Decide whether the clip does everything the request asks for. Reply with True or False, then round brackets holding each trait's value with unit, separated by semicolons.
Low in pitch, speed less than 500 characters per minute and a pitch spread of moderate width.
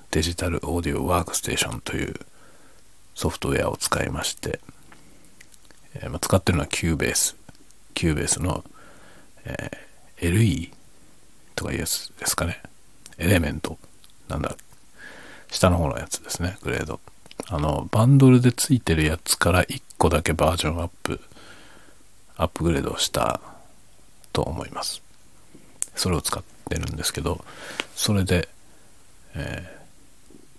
True (85 Hz; 285 characters per minute; 3.5 semitones)